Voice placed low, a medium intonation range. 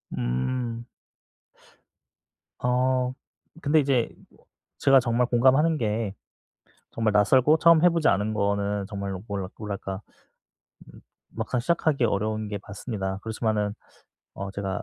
Yes: low, 110 Hz; average, 4.1 semitones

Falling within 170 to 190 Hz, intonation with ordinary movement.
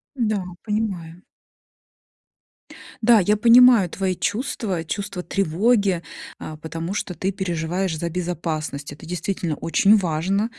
Yes: medium, 185 Hz; average, 3.9 semitones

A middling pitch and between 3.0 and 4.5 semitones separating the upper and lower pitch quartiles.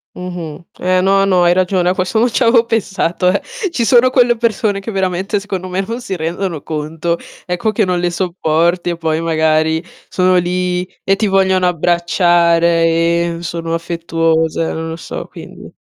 No: medium, 180 Hz; narrow, 2.6 semitones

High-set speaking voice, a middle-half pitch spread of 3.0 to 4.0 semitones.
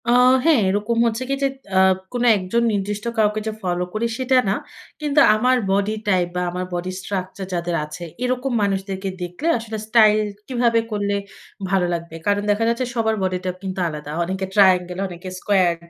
Yes: high, 200 Hz; average, 3.7 semitones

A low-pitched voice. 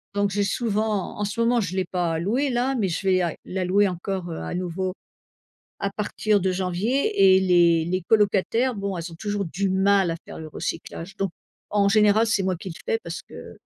No: high, 195 Hz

